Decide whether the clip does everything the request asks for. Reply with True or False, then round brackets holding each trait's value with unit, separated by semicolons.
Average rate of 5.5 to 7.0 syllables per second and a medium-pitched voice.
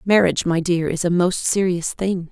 False (5.0 syllables/s; 180 Hz)